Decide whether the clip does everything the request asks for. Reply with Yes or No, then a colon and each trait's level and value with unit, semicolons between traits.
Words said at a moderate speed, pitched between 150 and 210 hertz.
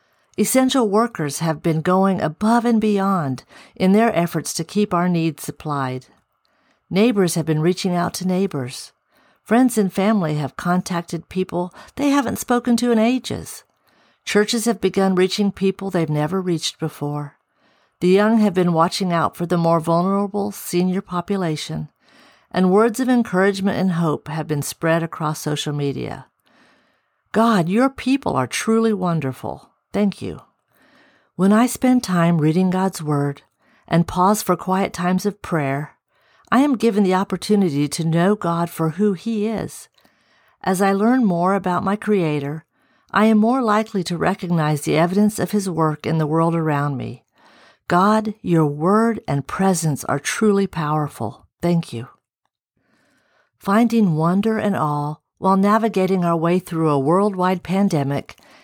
Yes: average, 150 wpm; medium, 185 Hz